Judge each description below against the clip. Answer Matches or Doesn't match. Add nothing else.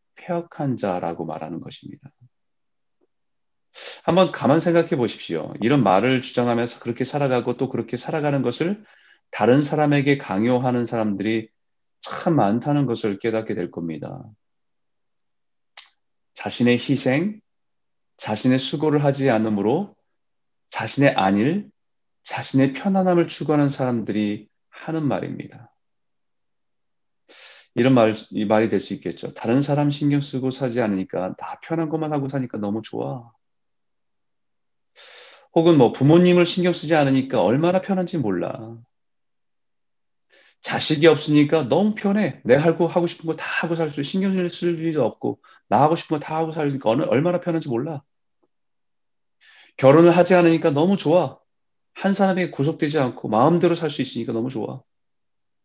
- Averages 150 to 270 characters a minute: Doesn't match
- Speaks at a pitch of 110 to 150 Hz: Matches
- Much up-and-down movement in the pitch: Matches